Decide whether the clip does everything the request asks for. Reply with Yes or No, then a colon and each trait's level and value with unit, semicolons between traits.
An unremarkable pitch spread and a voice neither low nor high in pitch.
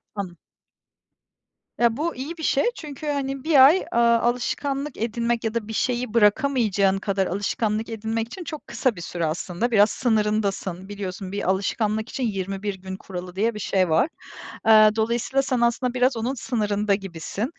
No: average, 4.0 semitones; high, 220 Hz